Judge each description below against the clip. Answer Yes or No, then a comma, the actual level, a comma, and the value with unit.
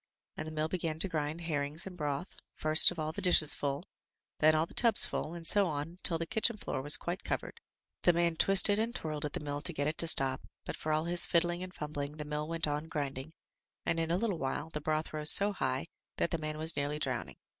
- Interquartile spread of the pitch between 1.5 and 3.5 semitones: Yes, narrow, 2.6 semitones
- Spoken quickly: Yes, fast, 245 wpm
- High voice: No, medium, 155 Hz